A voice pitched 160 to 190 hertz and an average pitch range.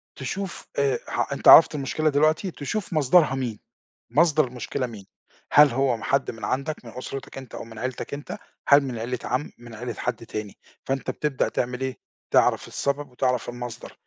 No: low, 130 Hz; average, 3.1 semitones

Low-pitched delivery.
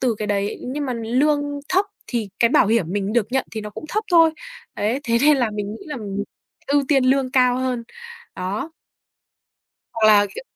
No: high, 245 Hz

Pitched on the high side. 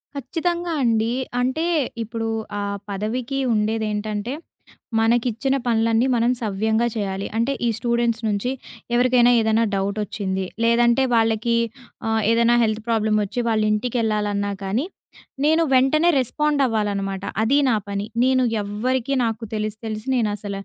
Yes: high, 225 Hz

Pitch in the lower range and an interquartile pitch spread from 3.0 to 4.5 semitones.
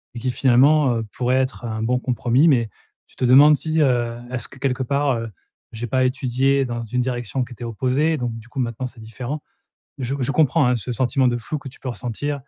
No: low, 125 Hz; narrow, 2.4 semitones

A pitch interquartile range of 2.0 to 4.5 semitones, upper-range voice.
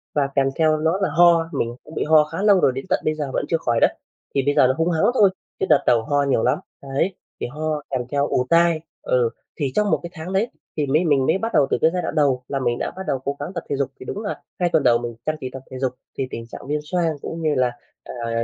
No: average, 4.0 semitones; medium, 150 Hz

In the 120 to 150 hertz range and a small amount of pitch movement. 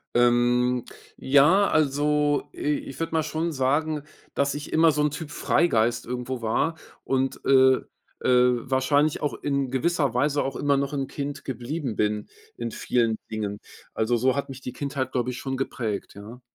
No: low, 135 Hz; average, 3.2 semitones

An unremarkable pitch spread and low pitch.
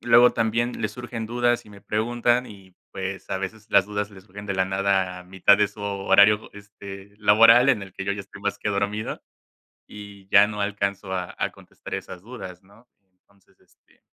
No: narrow, 1.9 semitones; low, 100 Hz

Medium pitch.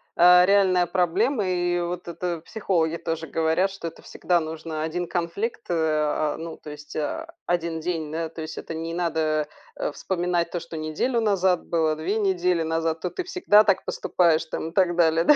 Yes: medium, 170 Hz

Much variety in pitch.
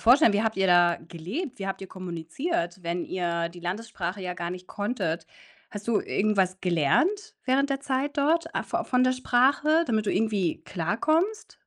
Yes: wide, 6.9 semitones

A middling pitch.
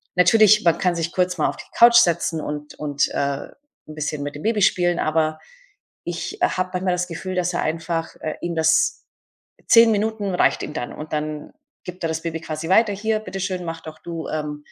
Yes: medium, 170 Hz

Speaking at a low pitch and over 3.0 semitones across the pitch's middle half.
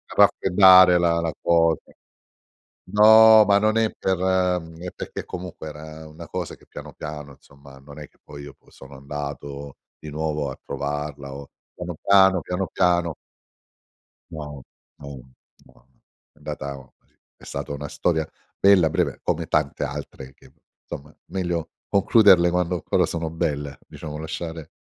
Yes: very low, 80 Hz; average, 3.9 semitones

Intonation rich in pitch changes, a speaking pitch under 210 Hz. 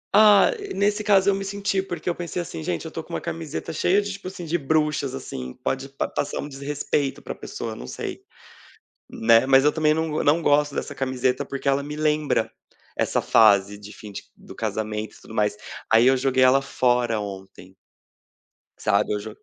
Yes: wide, 6.3 semitones; medium, 140 Hz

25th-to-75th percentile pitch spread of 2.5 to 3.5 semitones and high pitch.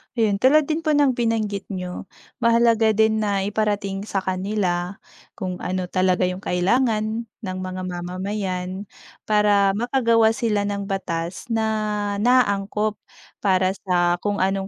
Yes: average, 2.9 semitones; high, 205 Hz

